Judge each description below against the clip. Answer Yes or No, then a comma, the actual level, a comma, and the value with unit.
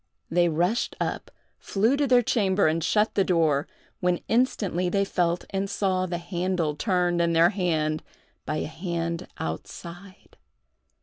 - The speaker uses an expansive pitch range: No, average, 2.7 semitones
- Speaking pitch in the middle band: Yes, medium, 180 Hz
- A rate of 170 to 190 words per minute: No, average, 145 wpm